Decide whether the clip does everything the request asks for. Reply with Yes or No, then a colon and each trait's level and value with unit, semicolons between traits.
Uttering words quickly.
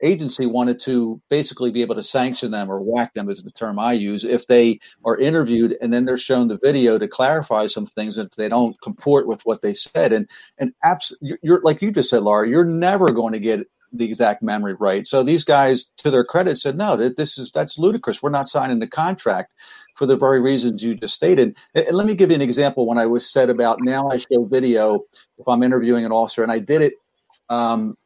Yes: fast, 235 wpm